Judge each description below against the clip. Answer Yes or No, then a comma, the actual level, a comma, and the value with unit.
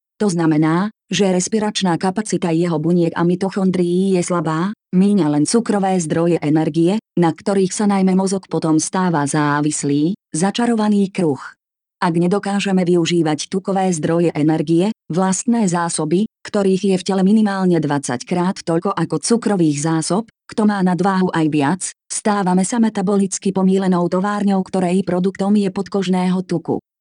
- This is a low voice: No, medium, 185 Hz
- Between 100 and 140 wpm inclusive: Yes, average, 135 wpm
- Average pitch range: Yes, average, 3.0 semitones